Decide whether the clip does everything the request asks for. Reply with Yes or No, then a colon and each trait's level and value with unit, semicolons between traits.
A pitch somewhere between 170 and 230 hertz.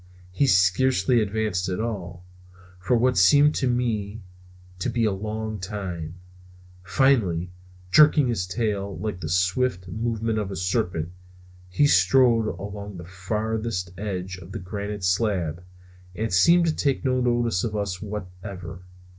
No: low, 100 Hz